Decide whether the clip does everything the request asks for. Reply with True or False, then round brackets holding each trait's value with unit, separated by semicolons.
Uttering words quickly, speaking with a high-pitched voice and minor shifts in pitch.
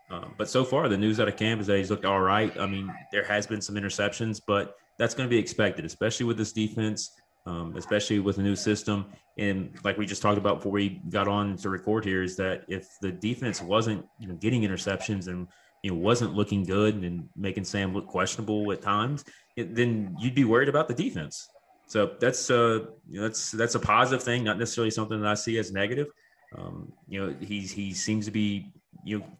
False (225 wpm; 105 Hz; 2.2 semitones)